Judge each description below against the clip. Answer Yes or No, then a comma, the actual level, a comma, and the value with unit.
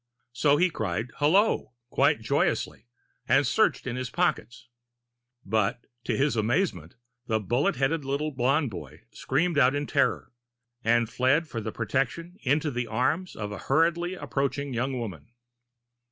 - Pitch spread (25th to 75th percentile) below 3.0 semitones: No, average, 4.5 semitones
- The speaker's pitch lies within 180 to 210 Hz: No, low, 135 Hz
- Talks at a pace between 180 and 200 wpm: No, average, 140 wpm